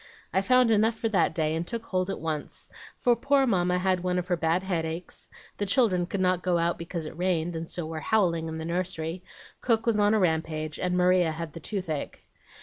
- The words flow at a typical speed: No, fast, 220 wpm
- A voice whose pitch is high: No, medium, 180 Hz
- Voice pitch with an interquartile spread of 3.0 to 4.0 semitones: Yes, average, 3.3 semitones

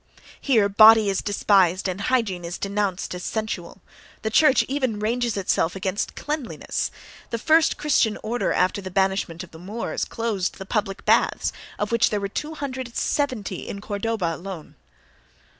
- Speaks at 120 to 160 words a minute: Yes, average, 150 wpm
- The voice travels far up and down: No, average, 3.5 semitones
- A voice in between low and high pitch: No, high, 205 Hz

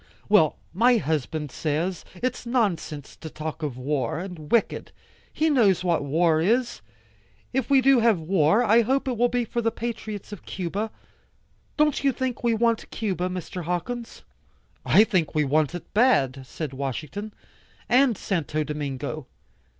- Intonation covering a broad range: Yes, wide, 7.2 semitones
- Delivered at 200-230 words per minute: No, average, 155 wpm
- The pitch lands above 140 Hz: Yes, medium, 185 Hz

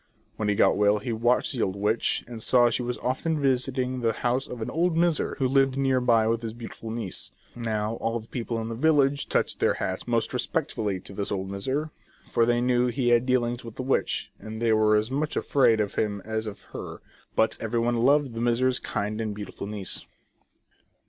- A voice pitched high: No, low, 120 Hz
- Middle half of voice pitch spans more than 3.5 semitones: No, average, 2.8 semitones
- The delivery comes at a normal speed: No, fast, 210 wpm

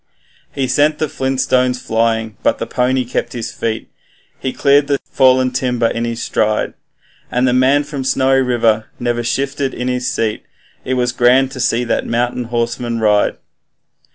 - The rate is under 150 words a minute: No, average, 170 wpm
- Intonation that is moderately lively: No, narrow, 2.0 semitones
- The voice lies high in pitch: No, low, 125 Hz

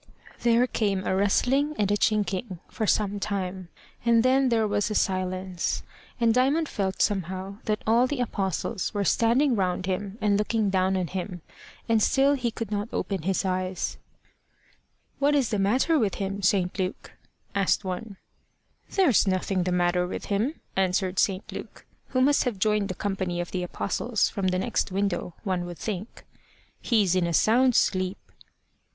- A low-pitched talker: No, high, 200 Hz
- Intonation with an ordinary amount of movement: Yes, average, 3.5 semitones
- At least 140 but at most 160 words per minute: No, average, 170 wpm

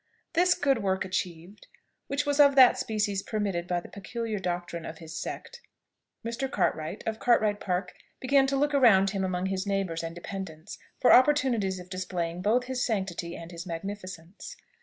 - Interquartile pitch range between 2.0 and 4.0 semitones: No, average, 5.2 semitones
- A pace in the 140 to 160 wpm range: No, average, 170 wpm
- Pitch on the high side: Yes, high, 195 Hz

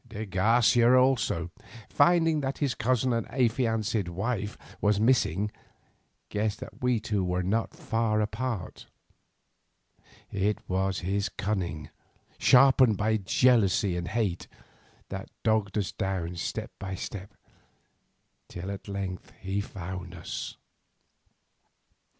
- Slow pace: Yes, slow, 115 wpm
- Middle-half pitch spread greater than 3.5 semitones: Yes, average, 3.9 semitones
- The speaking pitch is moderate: No, low, 105 Hz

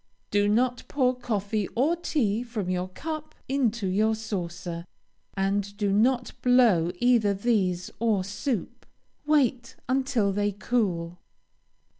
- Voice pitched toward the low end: No, high, 215 Hz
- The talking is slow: Yes, slow, 120 wpm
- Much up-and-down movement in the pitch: No, average, 4.2 semitones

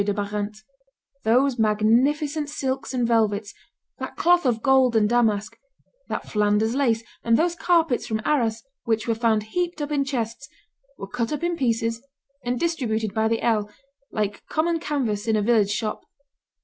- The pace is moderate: Yes, average, 160 wpm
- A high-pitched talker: Yes, high, 230 Hz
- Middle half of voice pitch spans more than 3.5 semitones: Yes, average, 4.3 semitones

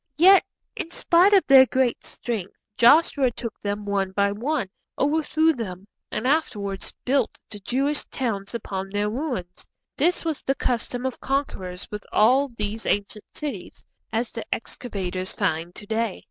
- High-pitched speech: Yes, high, 230 Hz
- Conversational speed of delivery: Yes, average, 150 wpm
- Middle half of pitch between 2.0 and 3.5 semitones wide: No, wide, 5.4 semitones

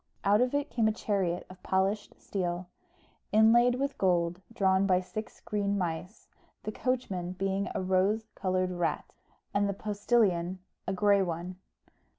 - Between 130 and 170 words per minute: Yes, average, 150 wpm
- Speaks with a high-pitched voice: Yes, high, 195 Hz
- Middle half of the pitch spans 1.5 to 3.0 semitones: Yes, average, 2.7 semitones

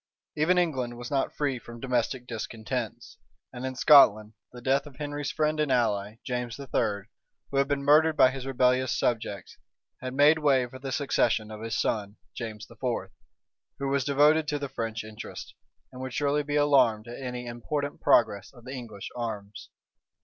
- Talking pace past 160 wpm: Yes, average, 175 wpm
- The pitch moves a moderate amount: Yes, average, 3.5 semitones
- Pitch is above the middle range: No, low, 130 Hz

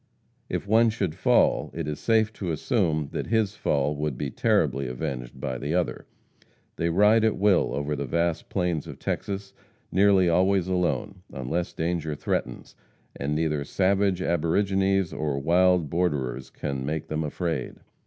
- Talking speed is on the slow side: No, average, 155 wpm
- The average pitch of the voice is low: Yes, very low, 85 Hz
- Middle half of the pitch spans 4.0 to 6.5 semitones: Yes, average, 4.7 semitones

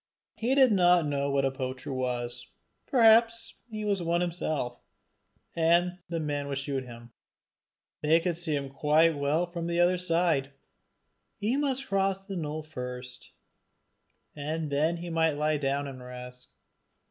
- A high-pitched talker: No, medium, 155 Hz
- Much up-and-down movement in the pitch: No, average, 4.4 semitones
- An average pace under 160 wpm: Yes, average, 150 wpm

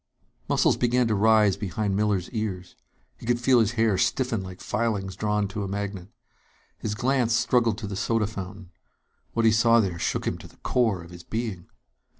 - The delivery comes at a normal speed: Yes, average, 185 wpm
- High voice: No, low, 105 Hz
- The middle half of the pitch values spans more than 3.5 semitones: No, average, 3.0 semitones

